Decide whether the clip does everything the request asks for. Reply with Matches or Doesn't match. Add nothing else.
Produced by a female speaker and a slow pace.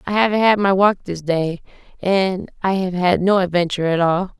Doesn't match